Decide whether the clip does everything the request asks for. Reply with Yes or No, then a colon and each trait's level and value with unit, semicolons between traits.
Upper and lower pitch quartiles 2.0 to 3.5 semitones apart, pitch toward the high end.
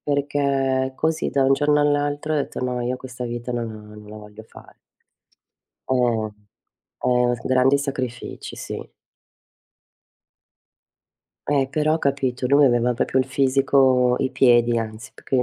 No: narrow, 2.4 semitones; low, 130 Hz